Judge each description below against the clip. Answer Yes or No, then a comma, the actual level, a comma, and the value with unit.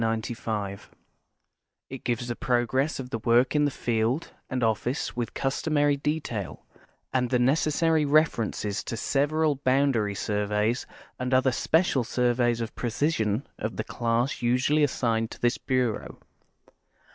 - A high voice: No, low, 125 Hz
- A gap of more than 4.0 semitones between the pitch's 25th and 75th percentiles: No, average, 3.6 semitones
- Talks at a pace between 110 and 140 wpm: Yes, slow, 135 wpm